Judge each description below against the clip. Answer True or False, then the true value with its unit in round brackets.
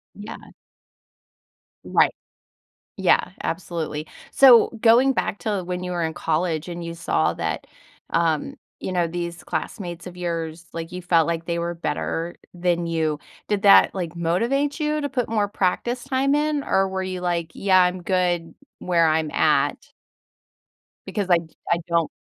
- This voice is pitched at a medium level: True (175 Hz)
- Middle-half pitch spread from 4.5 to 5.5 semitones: False (3.3 semitones)